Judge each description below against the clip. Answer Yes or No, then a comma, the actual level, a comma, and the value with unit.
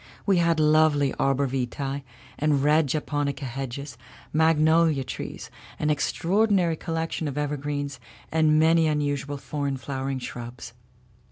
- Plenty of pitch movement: No, narrow, 2.5 semitones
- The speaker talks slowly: Yes, slow, 110 wpm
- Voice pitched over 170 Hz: No, medium, 145 Hz